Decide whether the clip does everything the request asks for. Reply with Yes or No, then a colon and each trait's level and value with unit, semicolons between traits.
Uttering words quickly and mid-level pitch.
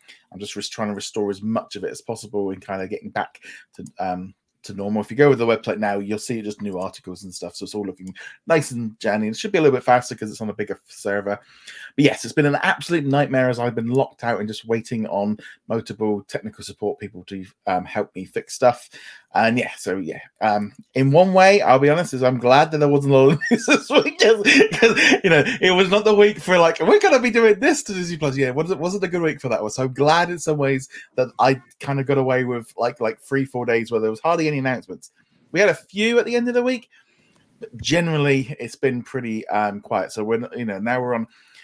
No: fast, 255 wpm; low, 125 Hz